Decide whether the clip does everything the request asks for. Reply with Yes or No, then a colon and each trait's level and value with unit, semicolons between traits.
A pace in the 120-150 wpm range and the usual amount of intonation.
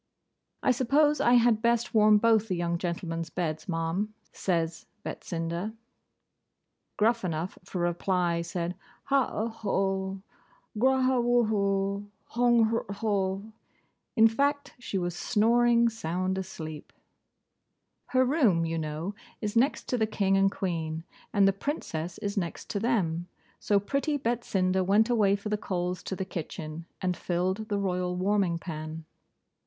Yes: slow, 135 wpm; average, 4.6 semitones